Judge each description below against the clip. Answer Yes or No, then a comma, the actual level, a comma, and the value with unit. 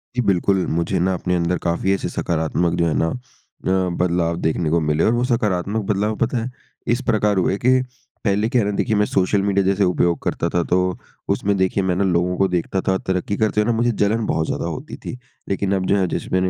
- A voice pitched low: Yes, very low, 95 Hz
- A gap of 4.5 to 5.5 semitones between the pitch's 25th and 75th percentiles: No, average, 2.8 semitones